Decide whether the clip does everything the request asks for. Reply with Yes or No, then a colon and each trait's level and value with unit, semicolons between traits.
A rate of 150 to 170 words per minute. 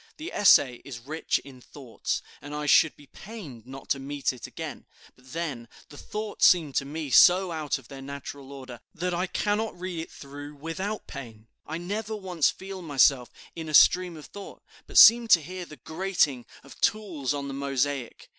No: average, 190 wpm